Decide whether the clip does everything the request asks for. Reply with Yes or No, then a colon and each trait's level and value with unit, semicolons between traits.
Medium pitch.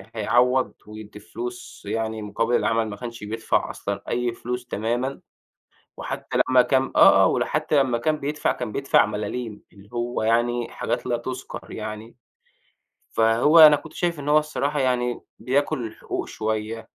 No: low, 120 Hz